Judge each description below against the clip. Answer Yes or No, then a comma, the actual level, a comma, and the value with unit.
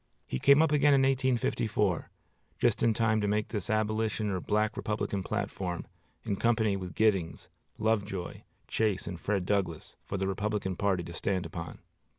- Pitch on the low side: Yes, low, 105 Hz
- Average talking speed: Yes, average, 165 wpm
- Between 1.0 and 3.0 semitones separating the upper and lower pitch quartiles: Yes, narrow, 2.6 semitones